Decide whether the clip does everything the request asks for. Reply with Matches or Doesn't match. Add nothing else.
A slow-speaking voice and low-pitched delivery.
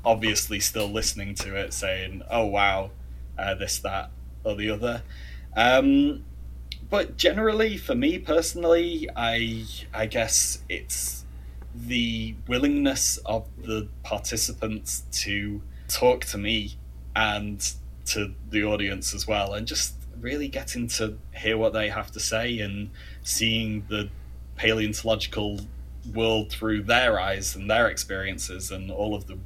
Matches